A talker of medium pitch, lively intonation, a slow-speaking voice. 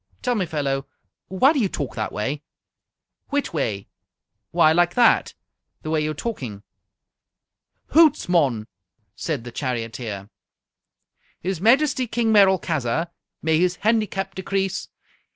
Yes: medium, 170 Hz; wide, 7.8 semitones; slow, 115 wpm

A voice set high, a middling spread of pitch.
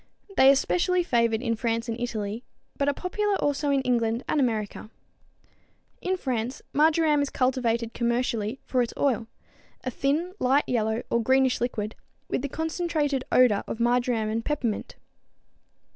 Yes: very high, 250 Hz; average, 3.8 semitones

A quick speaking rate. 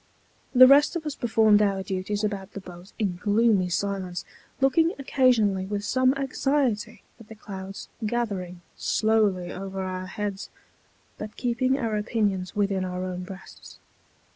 No: average, 140 wpm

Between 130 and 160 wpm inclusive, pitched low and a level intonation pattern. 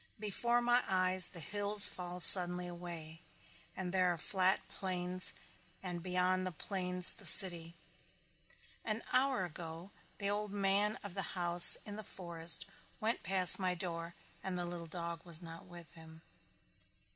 No: average, 155 wpm; medium, 180 Hz; narrow, 2.2 semitones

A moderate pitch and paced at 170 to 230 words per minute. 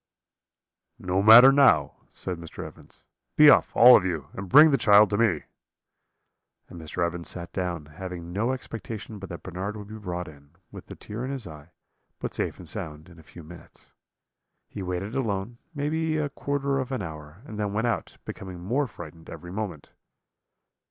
No: low, 100 Hz; average, 185 wpm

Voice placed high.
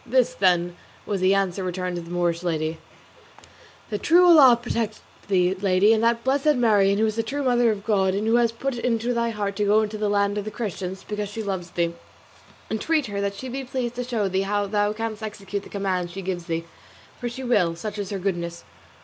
Yes: high, 205 Hz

